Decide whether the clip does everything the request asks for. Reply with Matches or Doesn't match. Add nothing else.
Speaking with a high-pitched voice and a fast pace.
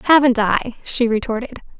Doesn't match